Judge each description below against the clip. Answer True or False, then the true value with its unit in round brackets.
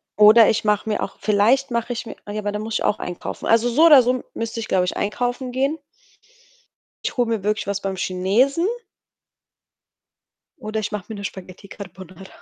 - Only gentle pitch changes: False (3.3 semitones)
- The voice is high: True (215 Hz)